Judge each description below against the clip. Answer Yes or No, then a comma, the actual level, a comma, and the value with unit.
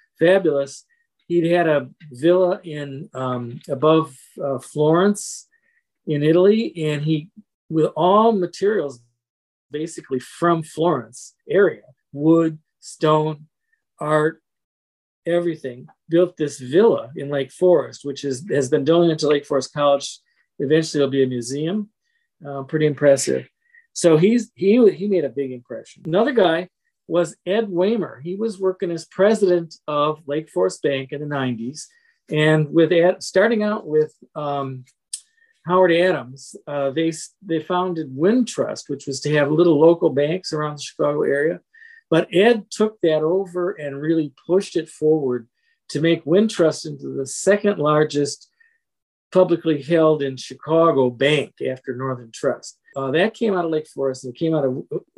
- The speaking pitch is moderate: Yes, medium, 160 Hz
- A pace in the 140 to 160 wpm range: Yes, average, 150 wpm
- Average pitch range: Yes, average, 4.8 semitones